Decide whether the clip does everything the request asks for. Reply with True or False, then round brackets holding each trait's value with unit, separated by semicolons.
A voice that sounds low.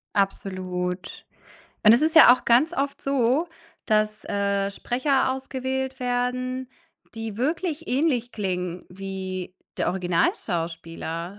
False (225 Hz)